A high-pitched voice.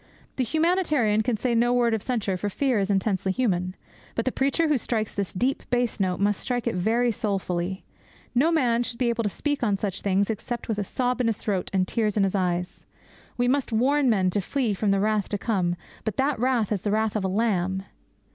Yes: high, 220 Hz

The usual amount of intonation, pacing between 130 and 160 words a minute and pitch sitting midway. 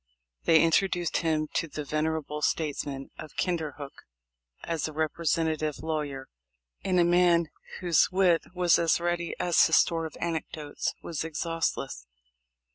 No: narrow, 2.0 semitones; average, 140 wpm; medium, 160 Hz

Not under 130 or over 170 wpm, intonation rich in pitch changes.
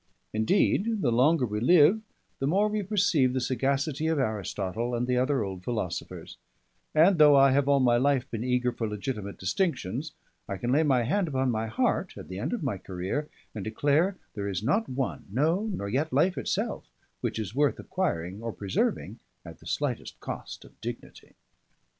No: average, 185 wpm; wide, 6.0 semitones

